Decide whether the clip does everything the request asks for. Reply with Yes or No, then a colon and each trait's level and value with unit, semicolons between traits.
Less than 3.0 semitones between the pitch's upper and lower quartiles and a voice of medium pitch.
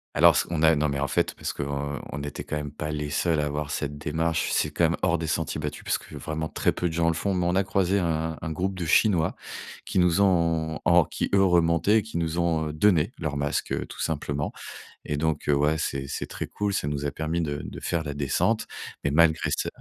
No: narrow, 2.6 semitones; very low, 80 Hz